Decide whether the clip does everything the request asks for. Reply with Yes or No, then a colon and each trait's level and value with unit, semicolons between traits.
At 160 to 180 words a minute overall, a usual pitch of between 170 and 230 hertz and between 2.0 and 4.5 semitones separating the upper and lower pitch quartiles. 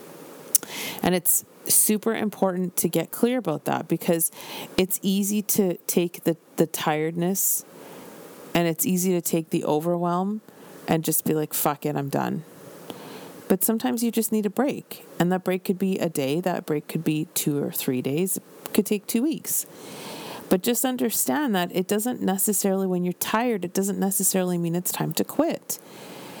Yes: average, 175 wpm; medium, 185 Hz; average, 4.0 semitones